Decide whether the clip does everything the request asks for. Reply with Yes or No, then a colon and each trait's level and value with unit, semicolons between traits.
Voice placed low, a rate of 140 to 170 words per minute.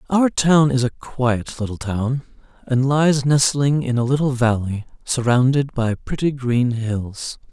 Yes: low, 130 Hz; average, 150 wpm